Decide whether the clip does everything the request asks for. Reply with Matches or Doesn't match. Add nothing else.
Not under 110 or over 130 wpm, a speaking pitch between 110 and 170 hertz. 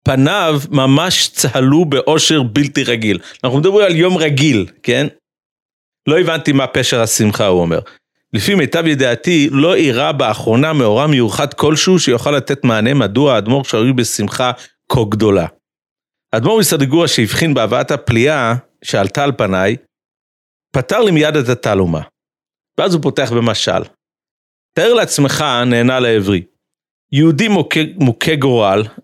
Matches